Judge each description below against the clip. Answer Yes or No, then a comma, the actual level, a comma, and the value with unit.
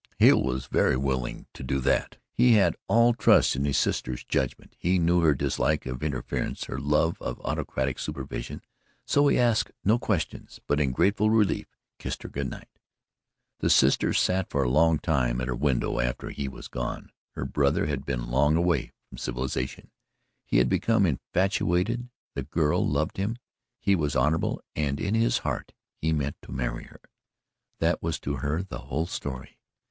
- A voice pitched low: Yes, very low, 75 Hz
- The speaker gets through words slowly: No, average, 175 wpm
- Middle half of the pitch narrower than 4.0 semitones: No, average, 5.2 semitones